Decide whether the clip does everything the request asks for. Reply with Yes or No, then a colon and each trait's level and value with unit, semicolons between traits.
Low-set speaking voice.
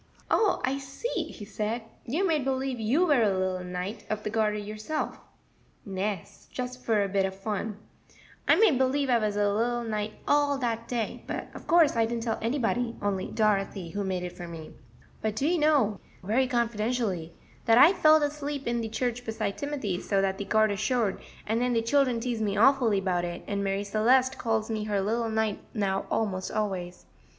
No: high, 220 Hz